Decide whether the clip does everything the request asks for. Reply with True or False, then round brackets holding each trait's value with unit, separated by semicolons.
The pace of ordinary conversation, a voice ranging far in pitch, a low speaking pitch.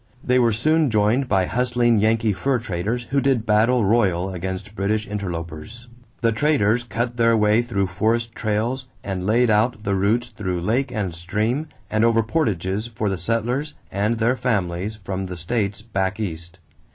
False (165 wpm; 3.6 semitones; 110 Hz)